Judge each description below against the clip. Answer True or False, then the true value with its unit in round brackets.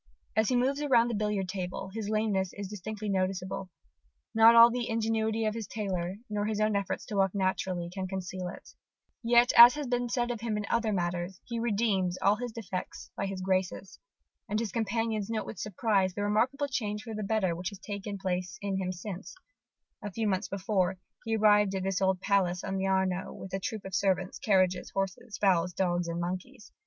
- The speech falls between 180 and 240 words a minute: True (200 wpm)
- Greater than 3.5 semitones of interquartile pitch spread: False (2.9 semitones)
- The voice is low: False (200 Hz)